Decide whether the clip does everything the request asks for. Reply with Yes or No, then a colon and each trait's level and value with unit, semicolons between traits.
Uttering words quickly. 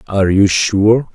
No: average, 160 wpm